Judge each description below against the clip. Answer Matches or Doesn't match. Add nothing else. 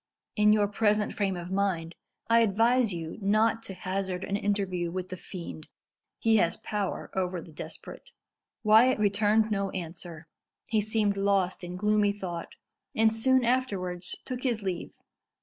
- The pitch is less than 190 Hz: Doesn't match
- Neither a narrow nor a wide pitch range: Matches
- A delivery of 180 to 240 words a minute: Doesn't match